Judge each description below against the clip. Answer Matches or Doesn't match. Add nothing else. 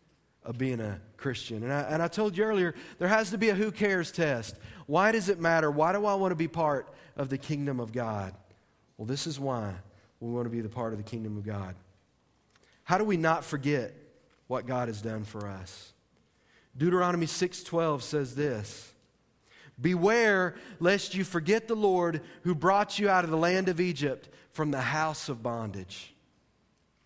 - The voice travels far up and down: Matches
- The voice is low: Doesn't match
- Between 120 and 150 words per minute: Doesn't match